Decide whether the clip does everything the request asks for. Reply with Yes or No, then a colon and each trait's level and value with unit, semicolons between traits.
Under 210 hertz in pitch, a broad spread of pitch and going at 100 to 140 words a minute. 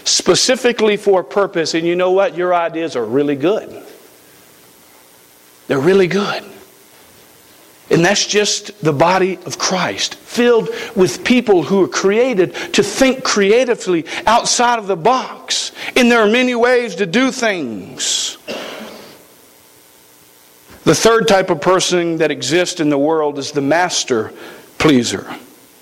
Yes: medium, 185 Hz; wide, 7.5 semitones; slow, 135 wpm